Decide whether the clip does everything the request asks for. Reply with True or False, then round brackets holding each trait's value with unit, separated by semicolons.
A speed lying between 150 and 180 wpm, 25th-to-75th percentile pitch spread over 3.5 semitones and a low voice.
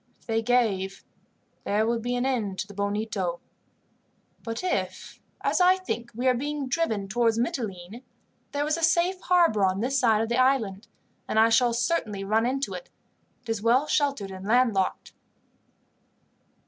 False (160 wpm; 4.5 semitones; 235 Hz)